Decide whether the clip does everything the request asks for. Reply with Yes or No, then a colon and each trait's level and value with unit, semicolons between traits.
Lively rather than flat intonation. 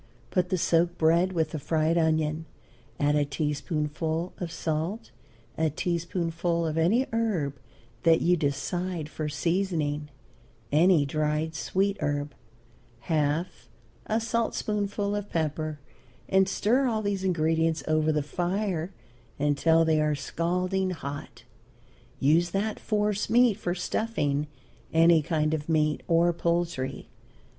No: average, 3.4 semitones